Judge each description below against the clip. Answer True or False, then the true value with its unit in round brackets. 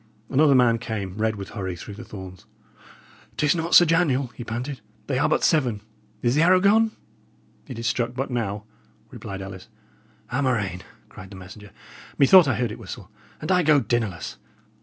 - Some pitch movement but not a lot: False (5.8 semitones)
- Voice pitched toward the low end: True (120 Hz)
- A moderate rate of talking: True (175 wpm)